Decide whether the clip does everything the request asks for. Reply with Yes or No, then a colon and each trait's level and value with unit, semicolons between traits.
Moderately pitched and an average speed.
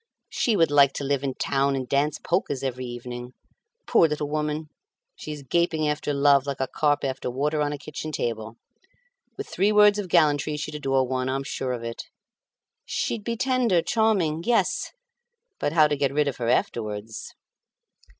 Yes: medium, 145 Hz; average, 180 wpm